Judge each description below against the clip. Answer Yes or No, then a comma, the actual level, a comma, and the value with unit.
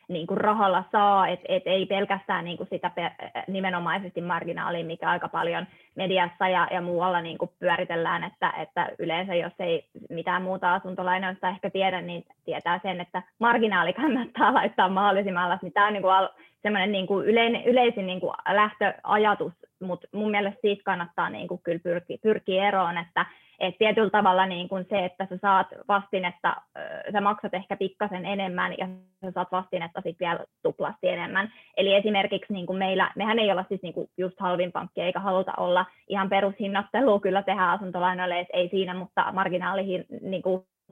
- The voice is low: No, high, 190 Hz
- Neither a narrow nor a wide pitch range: No, narrow, 1.8 semitones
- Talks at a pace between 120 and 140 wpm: No, fast, 155 wpm